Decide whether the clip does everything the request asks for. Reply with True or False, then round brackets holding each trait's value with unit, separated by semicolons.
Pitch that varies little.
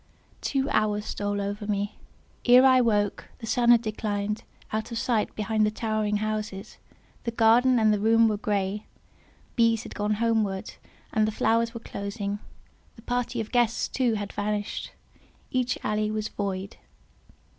True (1.9 semitones)